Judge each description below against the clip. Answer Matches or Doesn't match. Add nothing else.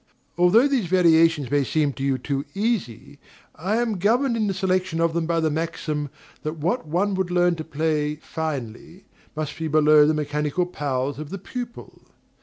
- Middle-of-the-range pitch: Matches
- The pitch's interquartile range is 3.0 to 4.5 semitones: Matches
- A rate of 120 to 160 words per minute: Doesn't match